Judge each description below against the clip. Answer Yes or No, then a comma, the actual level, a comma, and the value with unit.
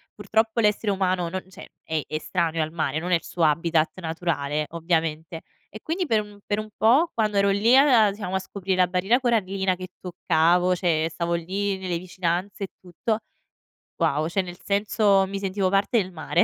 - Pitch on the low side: No, medium, 185 Hz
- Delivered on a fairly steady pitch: No, average, 3.4 semitones